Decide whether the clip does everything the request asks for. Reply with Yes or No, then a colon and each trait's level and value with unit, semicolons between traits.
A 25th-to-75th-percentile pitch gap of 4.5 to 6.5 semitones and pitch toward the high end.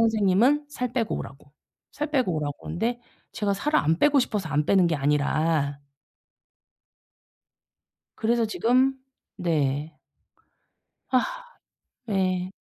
No: wide, 7.9 semitones; high, 195 Hz